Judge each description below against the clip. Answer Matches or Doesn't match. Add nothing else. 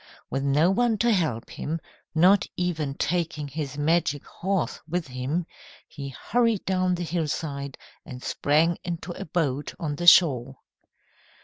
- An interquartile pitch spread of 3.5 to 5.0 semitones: Matches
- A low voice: Doesn't match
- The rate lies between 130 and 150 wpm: Matches